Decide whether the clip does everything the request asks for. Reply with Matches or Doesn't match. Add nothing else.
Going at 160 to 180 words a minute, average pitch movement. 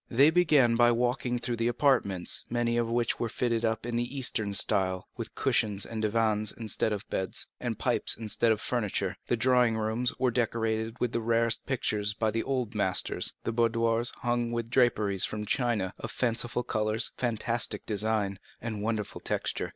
Doesn't match